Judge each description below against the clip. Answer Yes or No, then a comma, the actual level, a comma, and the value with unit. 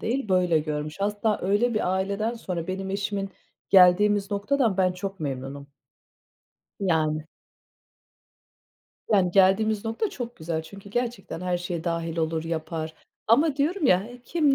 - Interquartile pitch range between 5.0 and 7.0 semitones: No, average, 4.4 semitones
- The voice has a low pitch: No, high, 195 Hz